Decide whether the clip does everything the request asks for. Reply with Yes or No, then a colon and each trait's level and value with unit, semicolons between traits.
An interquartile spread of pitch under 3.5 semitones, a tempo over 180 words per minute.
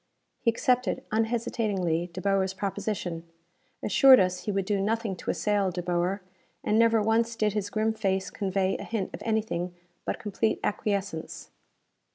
No: average, 2.8 semitones; average, 155 wpm